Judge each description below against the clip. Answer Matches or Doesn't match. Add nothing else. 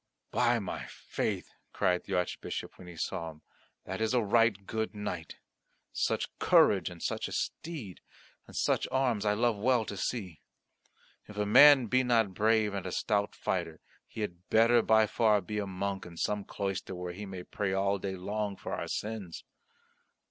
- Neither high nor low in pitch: Doesn't match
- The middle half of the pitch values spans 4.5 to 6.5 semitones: Doesn't match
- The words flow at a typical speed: Matches